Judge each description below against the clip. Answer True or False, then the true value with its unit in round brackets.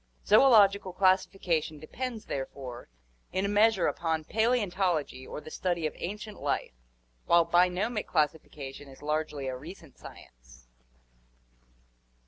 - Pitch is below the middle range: False (170 Hz)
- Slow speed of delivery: True (110 wpm)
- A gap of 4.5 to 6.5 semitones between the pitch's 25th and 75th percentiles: True (5.3 semitones)